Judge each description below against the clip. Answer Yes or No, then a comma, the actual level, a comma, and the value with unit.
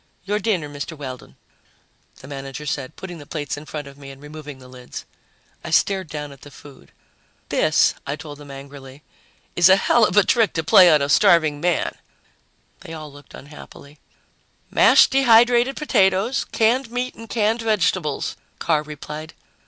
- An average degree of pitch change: No, wide, 5.8 semitones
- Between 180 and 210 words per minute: No, average, 170 wpm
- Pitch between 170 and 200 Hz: No, medium, 155 Hz